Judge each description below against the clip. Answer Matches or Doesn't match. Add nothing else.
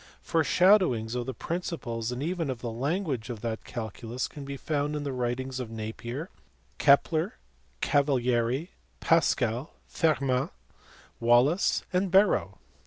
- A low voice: Matches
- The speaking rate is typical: Doesn't match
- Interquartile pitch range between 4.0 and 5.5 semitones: Matches